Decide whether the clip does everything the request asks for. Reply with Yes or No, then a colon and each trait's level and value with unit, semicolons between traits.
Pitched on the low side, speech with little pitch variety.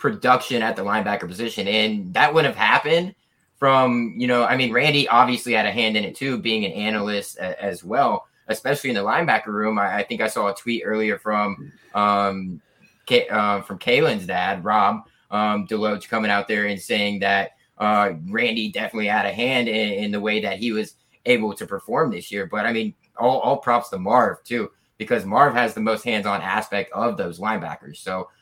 No: low, 110 Hz; average, 3.2 semitones